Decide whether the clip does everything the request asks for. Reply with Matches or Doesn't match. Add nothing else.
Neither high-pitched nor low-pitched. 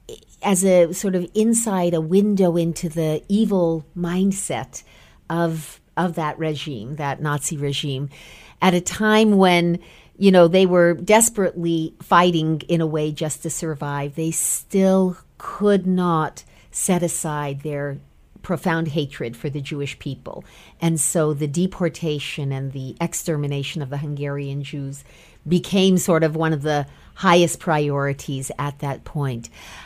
Matches